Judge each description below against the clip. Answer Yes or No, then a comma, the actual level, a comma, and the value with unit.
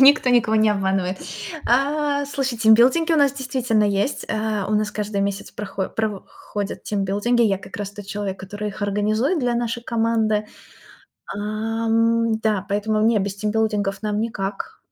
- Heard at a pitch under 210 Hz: No, high, 215 Hz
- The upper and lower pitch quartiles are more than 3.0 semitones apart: No, narrow, 2.6 semitones